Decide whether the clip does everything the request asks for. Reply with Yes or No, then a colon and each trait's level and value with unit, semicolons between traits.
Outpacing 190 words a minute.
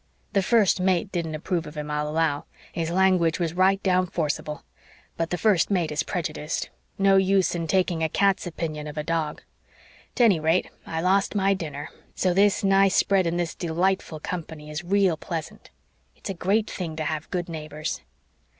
No: average, 180 wpm